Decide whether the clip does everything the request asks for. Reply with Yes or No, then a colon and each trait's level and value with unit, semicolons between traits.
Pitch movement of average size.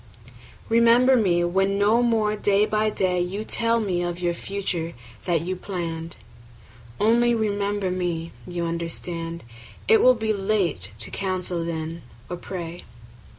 Yes: average, 3.9 semitones